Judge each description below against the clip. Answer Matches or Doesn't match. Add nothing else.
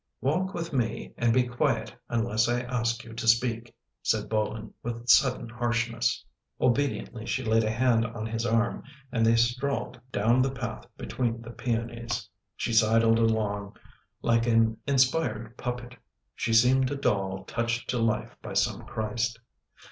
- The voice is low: Matches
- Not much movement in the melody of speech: Matches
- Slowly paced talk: Doesn't match